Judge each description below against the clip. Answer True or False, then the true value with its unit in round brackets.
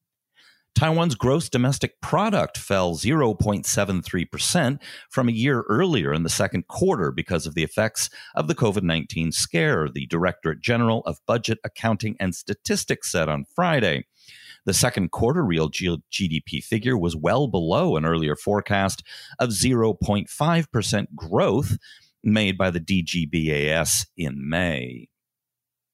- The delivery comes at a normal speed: False (125 wpm)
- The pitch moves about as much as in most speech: False (6.5 semitones)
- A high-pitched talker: False (100 Hz)